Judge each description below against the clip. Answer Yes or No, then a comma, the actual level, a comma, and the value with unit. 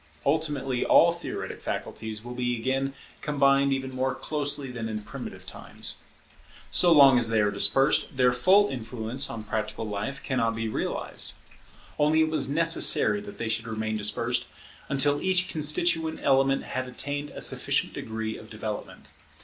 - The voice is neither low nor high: No, low, 130 Hz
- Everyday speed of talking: Yes, average, 155 wpm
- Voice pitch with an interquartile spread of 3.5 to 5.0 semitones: Yes, average, 4.3 semitones